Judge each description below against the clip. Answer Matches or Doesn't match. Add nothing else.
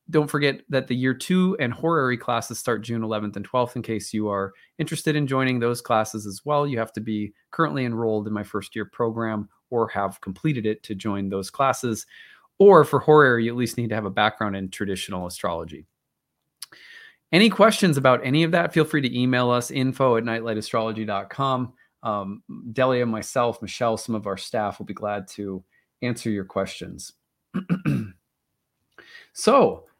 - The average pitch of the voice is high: Doesn't match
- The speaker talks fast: Doesn't match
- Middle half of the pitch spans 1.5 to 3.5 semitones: Doesn't match